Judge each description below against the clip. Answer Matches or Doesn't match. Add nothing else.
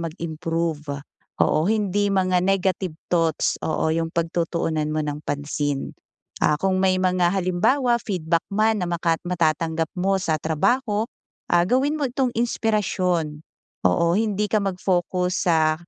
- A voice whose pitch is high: Doesn't match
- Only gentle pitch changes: Doesn't match